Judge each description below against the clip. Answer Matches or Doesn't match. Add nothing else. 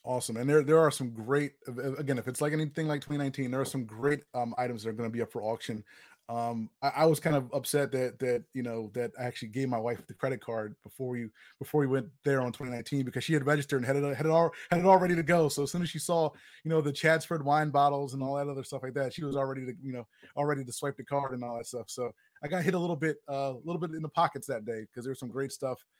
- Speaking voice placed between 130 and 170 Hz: Matches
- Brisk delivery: Matches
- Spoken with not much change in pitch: Doesn't match